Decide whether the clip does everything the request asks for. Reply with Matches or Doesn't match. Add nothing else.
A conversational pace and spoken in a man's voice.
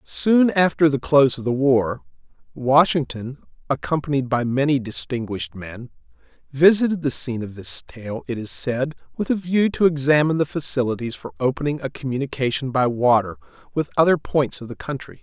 Matches